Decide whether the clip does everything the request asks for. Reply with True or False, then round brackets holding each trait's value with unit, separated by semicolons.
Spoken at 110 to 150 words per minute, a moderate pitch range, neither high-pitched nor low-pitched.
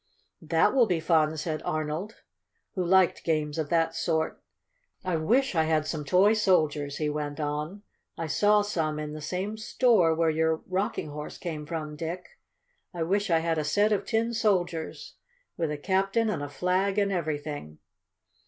False (170 wpm; 4.1 semitones; 165 Hz)